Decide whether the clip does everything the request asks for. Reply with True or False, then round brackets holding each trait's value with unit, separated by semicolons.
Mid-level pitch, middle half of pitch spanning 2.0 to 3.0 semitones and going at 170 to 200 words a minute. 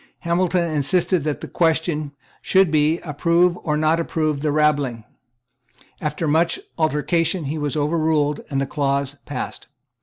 False (155 Hz; 2.4 semitones; 140 wpm)